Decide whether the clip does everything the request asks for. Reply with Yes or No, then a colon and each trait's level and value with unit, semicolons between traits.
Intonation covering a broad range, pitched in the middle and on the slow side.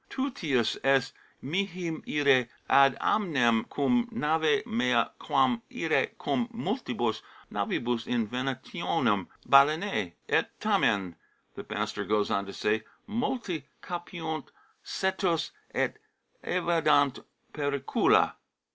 Yes: wide, 6.9 semitones; medium, 150 Hz; slow, 100 wpm